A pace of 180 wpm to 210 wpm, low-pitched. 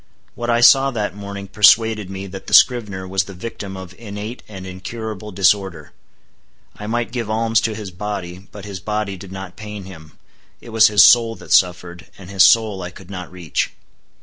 Yes: average, 190 wpm; low, 100 Hz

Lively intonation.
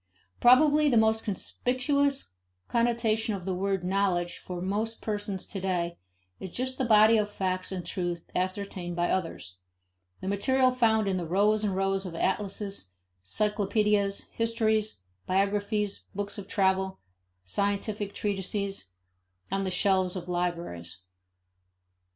No: average, 2.7 semitones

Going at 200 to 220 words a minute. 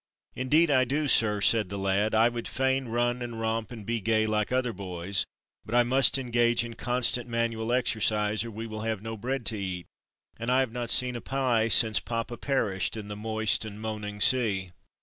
Yes: fast, 205 wpm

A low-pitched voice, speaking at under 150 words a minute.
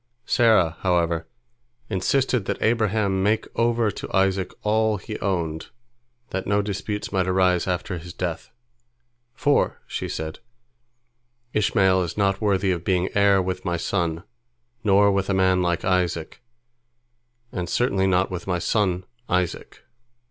Yes: very low, 95 Hz; slow, 135 wpm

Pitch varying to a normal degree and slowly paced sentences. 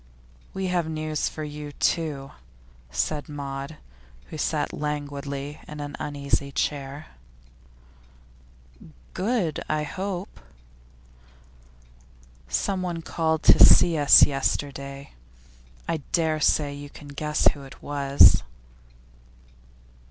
No: narrow, 2.1 semitones; slow, 100 wpm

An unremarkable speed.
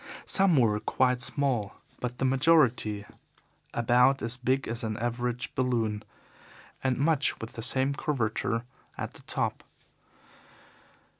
No: slow, 125 wpm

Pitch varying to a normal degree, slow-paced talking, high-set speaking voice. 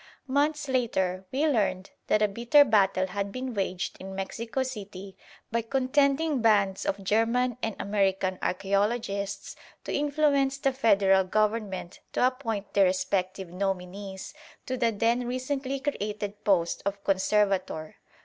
Yes: average, 4.8 semitones; slow, 130 wpm; high, 210 Hz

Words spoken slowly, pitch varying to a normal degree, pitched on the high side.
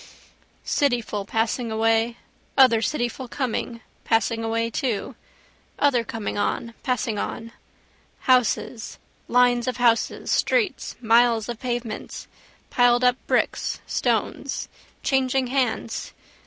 No: slow, 100 wpm; narrow, 2.0 semitones; high, 240 Hz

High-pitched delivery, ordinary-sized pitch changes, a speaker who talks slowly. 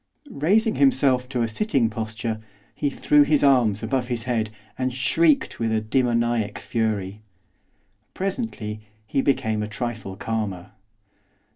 No: low, 120 Hz; average, 4.0 semitones; slow, 130 wpm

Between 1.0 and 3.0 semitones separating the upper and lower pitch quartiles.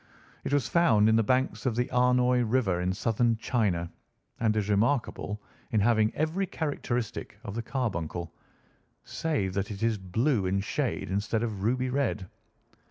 No: average, 3.9 semitones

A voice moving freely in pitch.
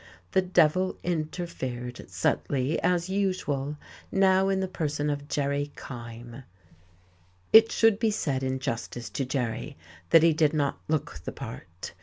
Yes: wide, 5.7 semitones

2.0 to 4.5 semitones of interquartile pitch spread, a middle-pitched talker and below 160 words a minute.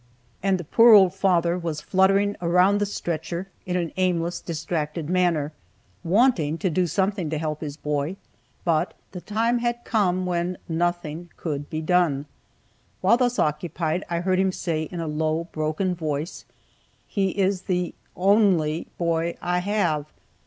Yes: average, 3.2 semitones; medium, 175 Hz; average, 150 wpm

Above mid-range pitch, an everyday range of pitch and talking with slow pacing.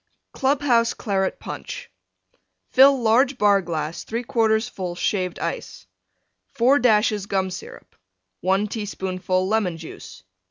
Yes: high, 210 Hz; average, 4.2 semitones; slow, 115 wpm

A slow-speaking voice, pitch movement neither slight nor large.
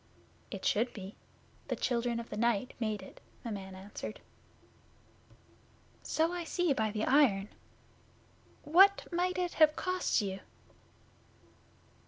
No: slow, 125 wpm; wide, 8.2 semitones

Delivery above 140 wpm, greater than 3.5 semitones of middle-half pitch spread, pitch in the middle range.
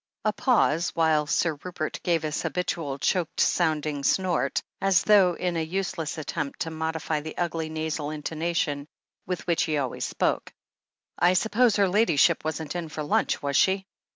No: average, 160 wpm; average, 2.8 semitones; medium, 160 Hz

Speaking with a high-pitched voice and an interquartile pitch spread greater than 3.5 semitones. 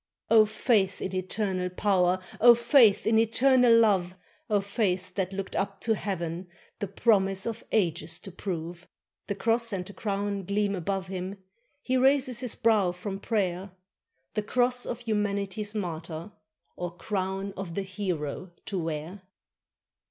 No: high, 195 Hz; average, 3.1 semitones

